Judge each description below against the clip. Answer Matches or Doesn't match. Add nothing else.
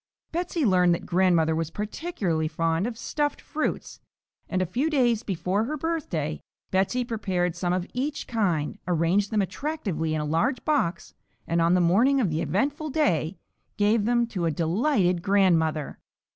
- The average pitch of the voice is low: Doesn't match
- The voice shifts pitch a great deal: Matches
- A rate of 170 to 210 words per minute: Doesn't match